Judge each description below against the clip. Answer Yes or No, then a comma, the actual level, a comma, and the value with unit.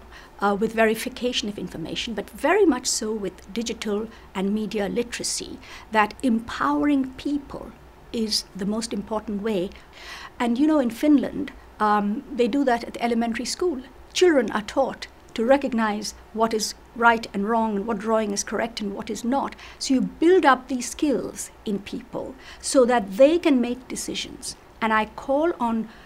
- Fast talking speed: No, average, 165 wpm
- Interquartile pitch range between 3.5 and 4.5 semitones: Yes, average, 3.8 semitones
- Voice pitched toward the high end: Yes, high, 235 Hz